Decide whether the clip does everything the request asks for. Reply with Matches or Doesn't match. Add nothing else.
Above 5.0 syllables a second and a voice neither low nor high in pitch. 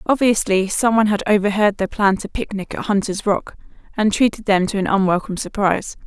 Doesn't match